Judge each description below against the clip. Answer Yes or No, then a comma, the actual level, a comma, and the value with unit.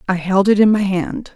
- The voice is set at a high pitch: Yes, high, 195 Hz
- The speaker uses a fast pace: Yes, fast, 265 wpm